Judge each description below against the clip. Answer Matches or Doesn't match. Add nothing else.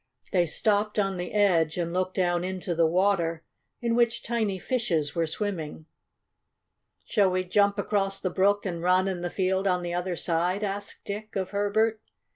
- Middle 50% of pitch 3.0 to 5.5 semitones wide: Doesn't match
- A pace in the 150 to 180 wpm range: Matches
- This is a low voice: Doesn't match